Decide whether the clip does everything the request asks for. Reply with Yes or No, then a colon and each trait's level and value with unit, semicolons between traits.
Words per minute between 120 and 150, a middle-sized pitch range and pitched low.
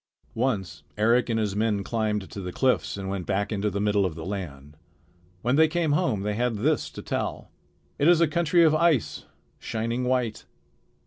No: average, 185 wpm; average, 5.0 semitones; low, 110 Hz